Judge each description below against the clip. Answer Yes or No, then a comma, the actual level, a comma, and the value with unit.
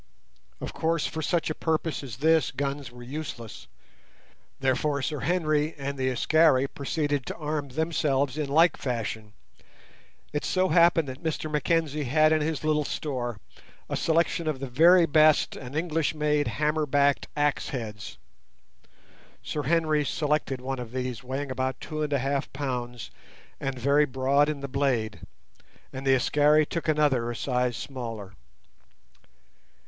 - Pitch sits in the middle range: Yes, medium, 145 Hz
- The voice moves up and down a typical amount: Yes, average, 3.0 semitones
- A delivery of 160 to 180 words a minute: No, average, 150 wpm